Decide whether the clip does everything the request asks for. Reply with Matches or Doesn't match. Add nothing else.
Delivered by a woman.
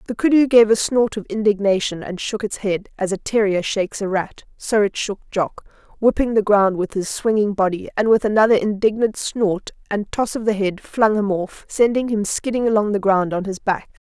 Matches